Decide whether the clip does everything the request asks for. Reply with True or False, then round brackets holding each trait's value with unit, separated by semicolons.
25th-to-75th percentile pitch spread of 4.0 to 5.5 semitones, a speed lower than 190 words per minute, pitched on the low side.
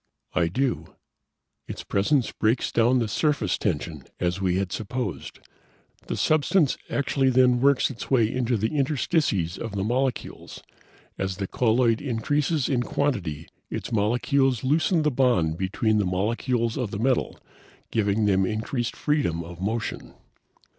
True (5.2 semitones; 140 wpm; 115 Hz)